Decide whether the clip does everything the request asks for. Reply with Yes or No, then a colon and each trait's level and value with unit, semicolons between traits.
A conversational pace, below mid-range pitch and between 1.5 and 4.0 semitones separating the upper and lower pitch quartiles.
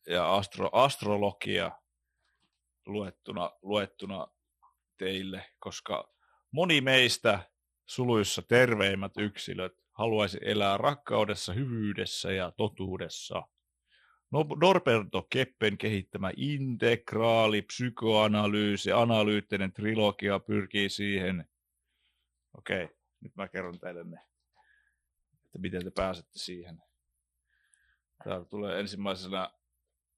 No: slow, 85 wpm; low, 100 Hz; average, 3.1 semitones